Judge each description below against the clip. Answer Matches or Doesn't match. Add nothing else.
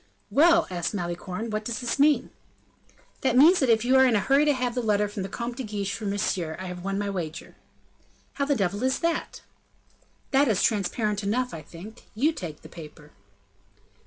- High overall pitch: Matches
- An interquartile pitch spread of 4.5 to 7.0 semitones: Matches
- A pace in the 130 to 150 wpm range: Doesn't match